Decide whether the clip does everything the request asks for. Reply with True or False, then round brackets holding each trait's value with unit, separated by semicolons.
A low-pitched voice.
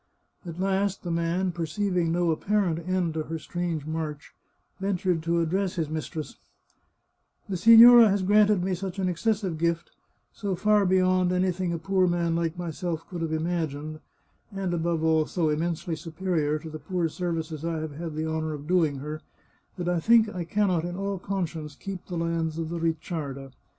False (170 Hz)